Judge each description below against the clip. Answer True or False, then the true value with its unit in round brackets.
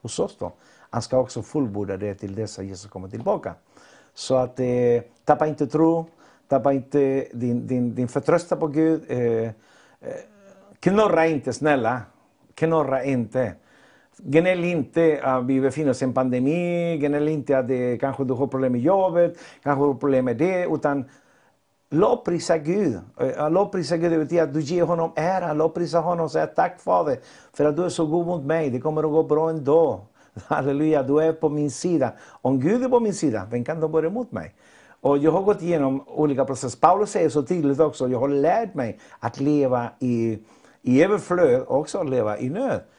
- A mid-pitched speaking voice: True (150 Hz)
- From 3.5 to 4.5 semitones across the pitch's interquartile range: True (4.2 semitones)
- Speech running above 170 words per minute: True (190 wpm)